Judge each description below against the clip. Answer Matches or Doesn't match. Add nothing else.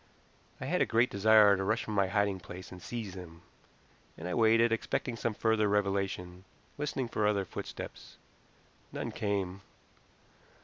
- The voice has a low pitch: Matches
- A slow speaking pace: Doesn't match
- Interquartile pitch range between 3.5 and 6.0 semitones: Doesn't match